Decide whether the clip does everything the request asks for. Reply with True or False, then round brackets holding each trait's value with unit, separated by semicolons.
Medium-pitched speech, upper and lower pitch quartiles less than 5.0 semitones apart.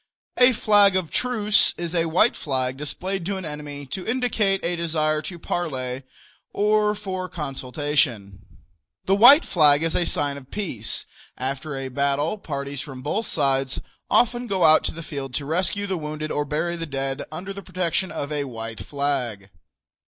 False (155 Hz; 5.4 semitones)